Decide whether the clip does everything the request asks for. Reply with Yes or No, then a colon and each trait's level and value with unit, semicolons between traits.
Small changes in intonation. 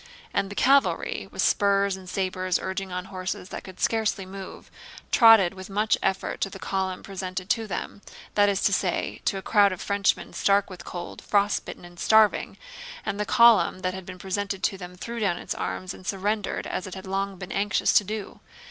Yes: narrow, 1.6 semitones